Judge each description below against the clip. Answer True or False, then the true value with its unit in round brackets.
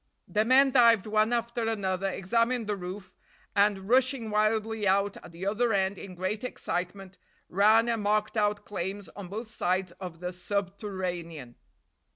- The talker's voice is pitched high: True (205 Hz)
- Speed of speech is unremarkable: True (155 wpm)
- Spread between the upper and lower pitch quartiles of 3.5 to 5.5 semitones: False (3.0 semitones)